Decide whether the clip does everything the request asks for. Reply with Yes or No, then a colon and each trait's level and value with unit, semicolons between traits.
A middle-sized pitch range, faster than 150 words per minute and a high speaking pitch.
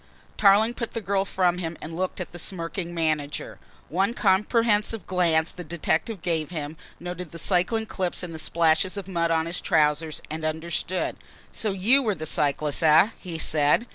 No: average, 3.3 semitones; average, 175 wpm; medium, 175 Hz